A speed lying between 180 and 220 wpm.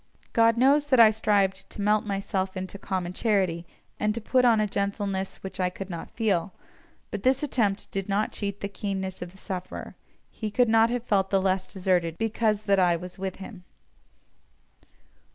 Yes: average, 185 wpm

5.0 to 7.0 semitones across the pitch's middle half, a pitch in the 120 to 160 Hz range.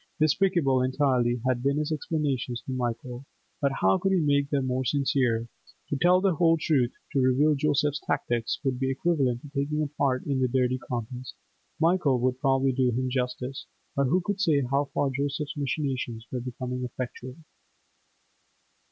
No: narrow, 2.6 semitones; low, 135 Hz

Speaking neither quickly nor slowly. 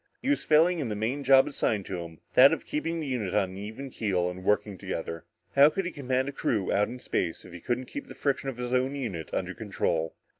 No: fast, 250 wpm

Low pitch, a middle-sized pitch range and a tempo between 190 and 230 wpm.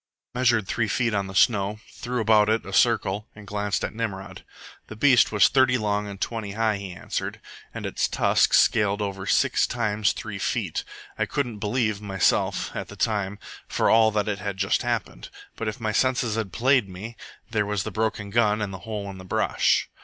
No: low, 105 Hz; narrow, 2.1 semitones; average, 200 wpm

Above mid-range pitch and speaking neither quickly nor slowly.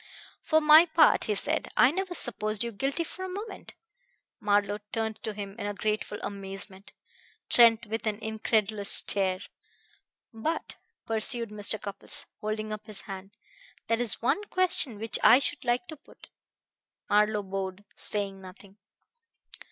Yes: high, 215 Hz; average, 145 wpm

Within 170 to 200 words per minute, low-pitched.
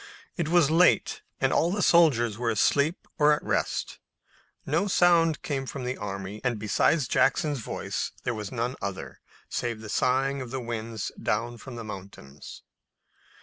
No: average, 160 wpm; low, 125 Hz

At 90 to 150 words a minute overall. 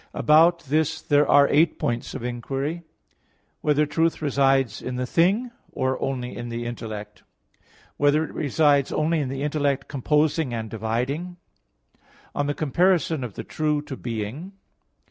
No: average, 160 wpm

